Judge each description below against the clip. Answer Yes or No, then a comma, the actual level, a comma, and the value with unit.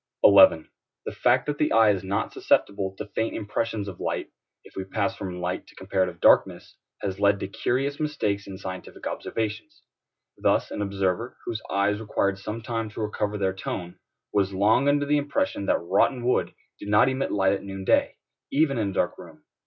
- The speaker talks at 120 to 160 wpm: No, average, 190 wpm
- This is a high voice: No, low, 100 Hz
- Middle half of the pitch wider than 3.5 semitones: No, average, 2.9 semitones